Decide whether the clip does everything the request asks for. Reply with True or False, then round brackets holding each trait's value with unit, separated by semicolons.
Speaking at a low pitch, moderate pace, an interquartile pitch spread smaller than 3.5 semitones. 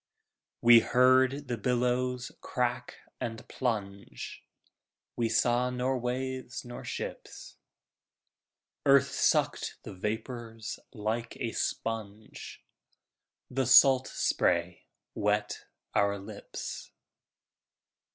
False (120 Hz; 85 wpm; 2.9 semitones)